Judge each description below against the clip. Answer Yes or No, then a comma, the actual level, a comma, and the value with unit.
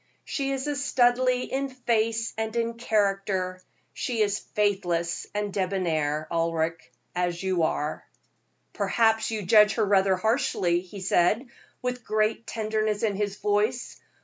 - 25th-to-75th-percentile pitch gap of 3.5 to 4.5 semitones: Yes, average, 3.8 semitones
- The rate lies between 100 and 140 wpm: Yes, slow, 135 wpm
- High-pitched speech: Yes, high, 210 Hz